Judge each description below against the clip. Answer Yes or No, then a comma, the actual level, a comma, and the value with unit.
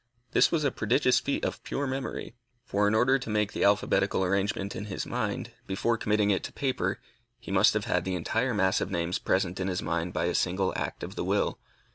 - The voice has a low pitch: Yes, low, 100 Hz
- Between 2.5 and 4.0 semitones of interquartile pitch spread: Yes, average, 3.7 semitones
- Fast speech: Yes, fast, 220 wpm